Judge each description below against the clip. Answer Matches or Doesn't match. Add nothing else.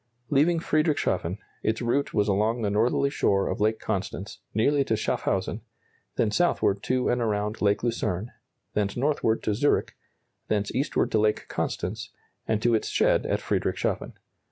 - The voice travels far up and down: Doesn't match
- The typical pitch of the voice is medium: Doesn't match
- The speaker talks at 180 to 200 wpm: Doesn't match